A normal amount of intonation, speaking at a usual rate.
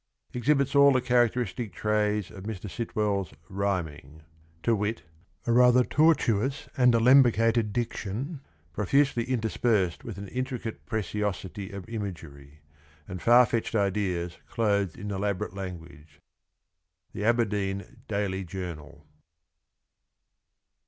No: average, 4.0 semitones; slow, 110 wpm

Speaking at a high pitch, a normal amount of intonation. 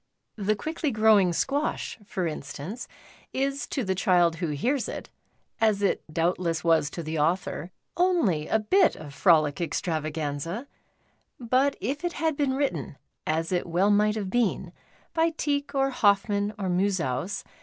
No: high, 200 Hz; wide, 7.7 semitones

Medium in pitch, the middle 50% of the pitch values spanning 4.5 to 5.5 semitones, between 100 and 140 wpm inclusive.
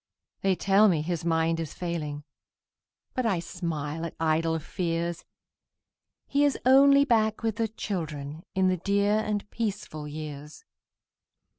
Yes: medium, 175 Hz; average, 4.8 semitones; slow, 135 wpm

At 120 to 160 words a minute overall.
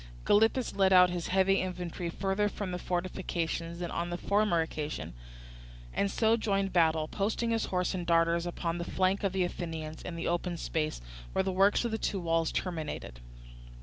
No: average, 180 wpm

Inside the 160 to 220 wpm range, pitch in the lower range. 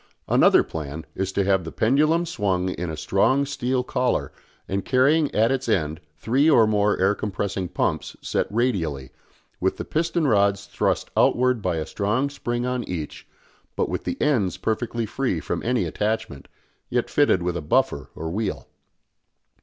Yes: average, 165 wpm; low, 105 Hz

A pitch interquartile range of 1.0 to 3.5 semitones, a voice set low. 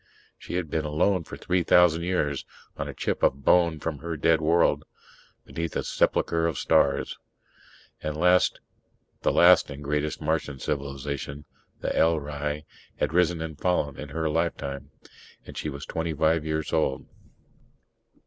Yes: narrow, 2.4 semitones; very low, 80 Hz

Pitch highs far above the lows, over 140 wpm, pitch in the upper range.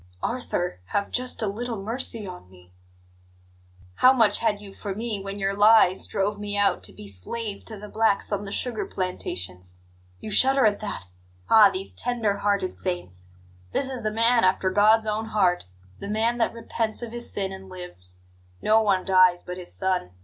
No: average, 3.4 semitones; average, 185 wpm; high, 205 Hz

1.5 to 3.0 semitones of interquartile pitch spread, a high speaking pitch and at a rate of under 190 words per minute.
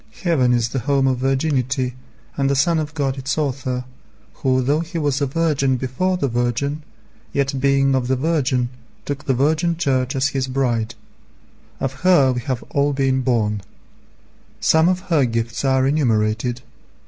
No: narrow, 2.4 semitones; low, 135 Hz; average, 165 wpm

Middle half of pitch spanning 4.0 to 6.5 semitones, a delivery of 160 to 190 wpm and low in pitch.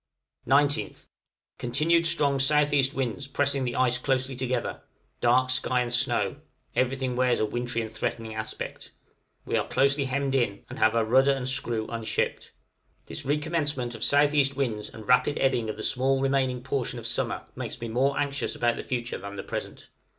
No: narrow, 2.6 semitones; average, 170 wpm; low, 130 Hz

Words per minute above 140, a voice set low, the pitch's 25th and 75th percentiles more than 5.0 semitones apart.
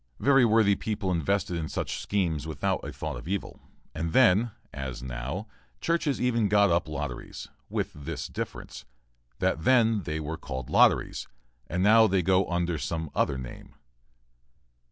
Yes: average, 155 wpm; very low, 90 Hz; wide, 5.4 semitones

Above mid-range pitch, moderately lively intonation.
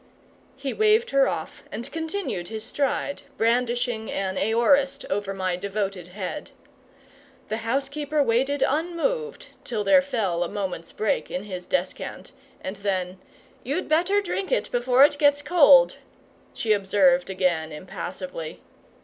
No: high, 235 Hz; wide, 7.0 semitones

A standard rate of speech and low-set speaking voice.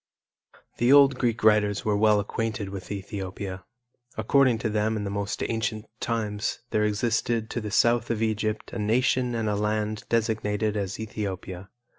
Yes: average, 160 wpm; low, 110 Hz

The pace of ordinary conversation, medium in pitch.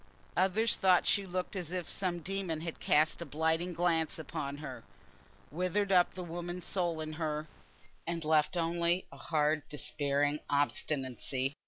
Yes: average, 150 wpm; medium, 165 Hz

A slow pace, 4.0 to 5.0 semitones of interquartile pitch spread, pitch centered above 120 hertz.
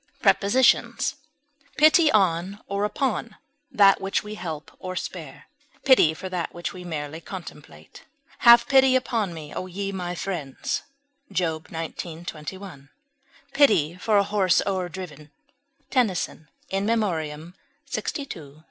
Yes: slow, 130 wpm; average, 4.5 semitones; medium, 185 Hz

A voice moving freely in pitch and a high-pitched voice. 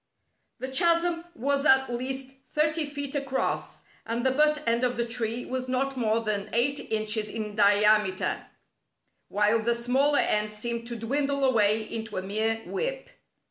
No: average, 4.1 semitones; high, 240 Hz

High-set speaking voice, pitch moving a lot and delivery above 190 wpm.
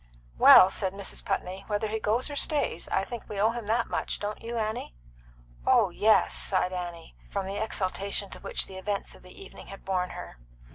No: high, 200 Hz; average, 2.7 semitones; average, 200 wpm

